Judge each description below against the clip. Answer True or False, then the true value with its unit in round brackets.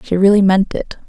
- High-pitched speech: True (195 Hz)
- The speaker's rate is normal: False (220 wpm)